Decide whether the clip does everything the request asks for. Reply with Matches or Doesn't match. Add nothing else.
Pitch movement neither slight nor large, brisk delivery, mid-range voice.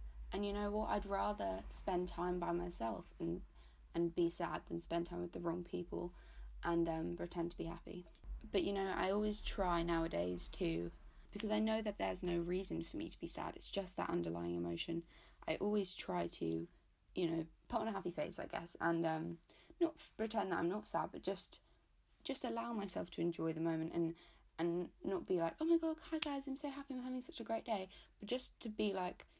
Matches